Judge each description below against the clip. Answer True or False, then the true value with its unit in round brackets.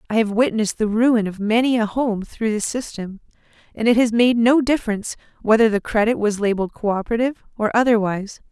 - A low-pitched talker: False (220 Hz)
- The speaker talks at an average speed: True (185 wpm)